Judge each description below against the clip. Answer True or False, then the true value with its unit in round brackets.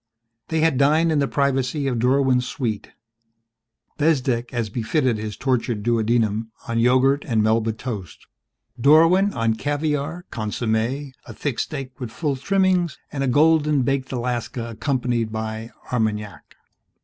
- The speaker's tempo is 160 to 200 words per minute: False (135 wpm)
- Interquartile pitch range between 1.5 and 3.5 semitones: False (4.1 semitones)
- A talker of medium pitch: False (125 Hz)